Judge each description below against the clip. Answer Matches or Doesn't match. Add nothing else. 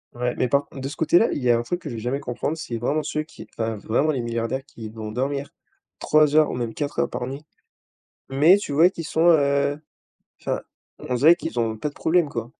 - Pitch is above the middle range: Doesn't match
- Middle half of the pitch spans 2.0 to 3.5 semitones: Doesn't match